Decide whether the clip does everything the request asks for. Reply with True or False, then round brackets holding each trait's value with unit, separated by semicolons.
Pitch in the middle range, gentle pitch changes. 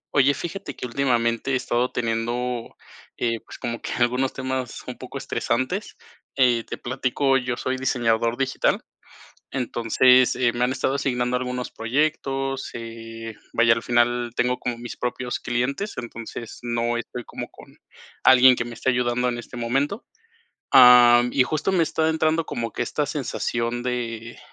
False (125 Hz; 1.8 semitones)